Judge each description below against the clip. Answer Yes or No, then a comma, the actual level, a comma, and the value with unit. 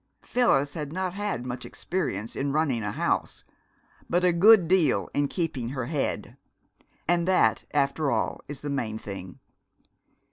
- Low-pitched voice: No, medium, 145 Hz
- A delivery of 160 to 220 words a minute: No, average, 150 wpm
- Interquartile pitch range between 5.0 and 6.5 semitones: Yes, wide, 5.5 semitones